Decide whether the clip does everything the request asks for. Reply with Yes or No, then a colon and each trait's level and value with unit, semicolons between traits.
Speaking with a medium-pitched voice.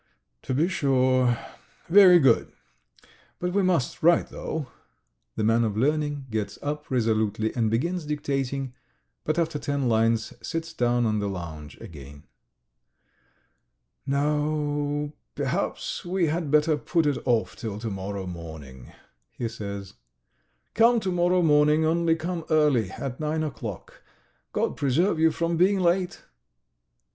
Yes: medium, 145 Hz